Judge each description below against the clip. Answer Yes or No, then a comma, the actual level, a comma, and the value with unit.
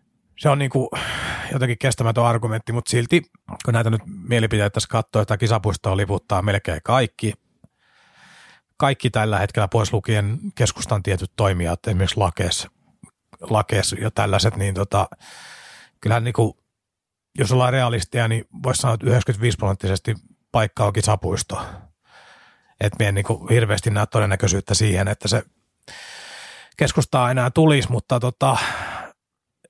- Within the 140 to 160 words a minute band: No, average, 125 wpm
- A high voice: No, low, 110 Hz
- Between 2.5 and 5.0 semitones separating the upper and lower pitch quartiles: Yes, average, 3.2 semitones